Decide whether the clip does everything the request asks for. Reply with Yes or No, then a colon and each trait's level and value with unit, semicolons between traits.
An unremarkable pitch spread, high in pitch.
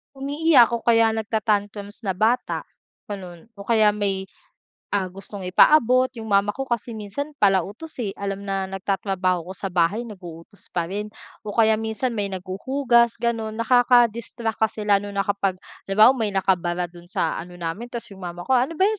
Yes: average, 3.5 semitones; high, 205 Hz